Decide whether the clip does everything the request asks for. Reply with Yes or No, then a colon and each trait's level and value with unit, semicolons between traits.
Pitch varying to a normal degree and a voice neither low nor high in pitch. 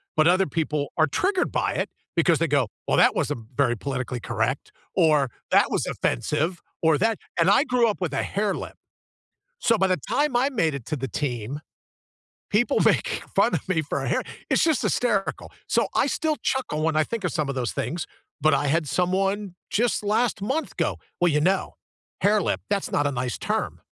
No: wide, 6.5 semitones; medium, 170 Hz